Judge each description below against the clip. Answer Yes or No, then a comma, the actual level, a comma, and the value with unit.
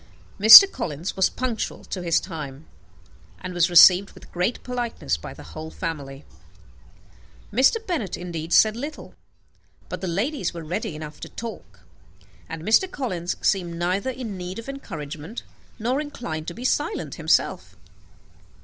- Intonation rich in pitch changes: Yes, wide, 6.6 semitones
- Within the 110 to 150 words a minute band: Yes, average, 145 wpm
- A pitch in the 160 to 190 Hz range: Yes, medium, 185 Hz